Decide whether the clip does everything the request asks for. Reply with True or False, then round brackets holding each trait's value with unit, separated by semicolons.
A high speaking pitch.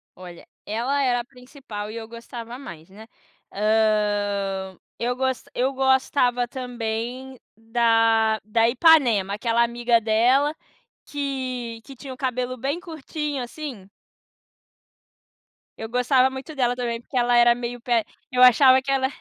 True (245 Hz)